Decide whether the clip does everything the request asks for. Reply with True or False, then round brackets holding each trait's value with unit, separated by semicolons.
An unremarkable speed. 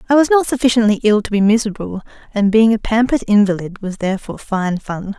True (195 wpm)